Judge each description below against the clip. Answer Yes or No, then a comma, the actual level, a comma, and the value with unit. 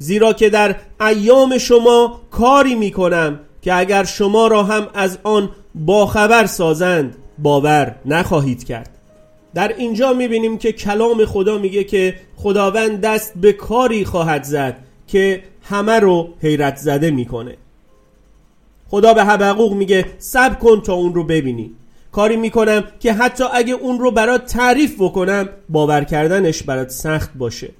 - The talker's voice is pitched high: Yes, high, 200 Hz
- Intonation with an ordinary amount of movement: No, wide, 5.9 semitones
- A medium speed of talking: Yes, average, 140 wpm